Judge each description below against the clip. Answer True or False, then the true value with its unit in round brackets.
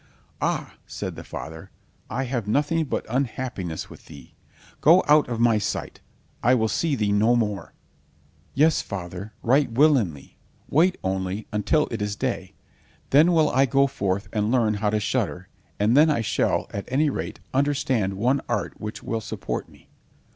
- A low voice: True (115 Hz)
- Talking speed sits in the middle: True (165 wpm)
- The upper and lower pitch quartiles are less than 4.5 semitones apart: False (5.3 semitones)